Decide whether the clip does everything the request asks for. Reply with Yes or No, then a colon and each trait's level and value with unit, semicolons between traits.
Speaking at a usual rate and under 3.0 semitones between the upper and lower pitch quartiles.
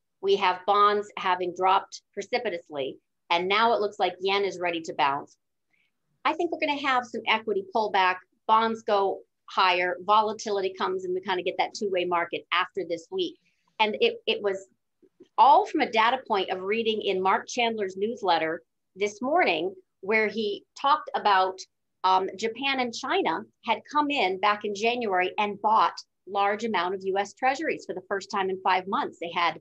No: average, 180 wpm; average, 3.6 semitones